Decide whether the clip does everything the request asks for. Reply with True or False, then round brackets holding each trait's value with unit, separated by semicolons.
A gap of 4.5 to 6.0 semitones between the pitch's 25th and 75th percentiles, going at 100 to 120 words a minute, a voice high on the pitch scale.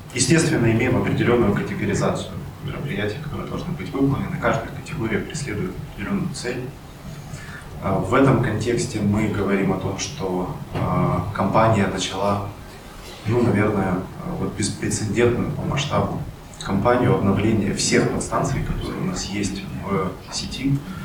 False (5.1 semitones; 110 wpm; 110 Hz)